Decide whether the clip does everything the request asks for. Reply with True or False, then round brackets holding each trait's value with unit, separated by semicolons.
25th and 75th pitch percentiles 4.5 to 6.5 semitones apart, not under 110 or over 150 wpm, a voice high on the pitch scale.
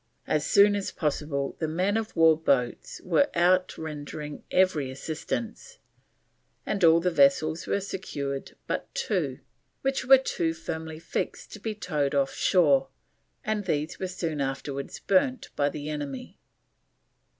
False (4.8 semitones; 140 wpm; 160 Hz)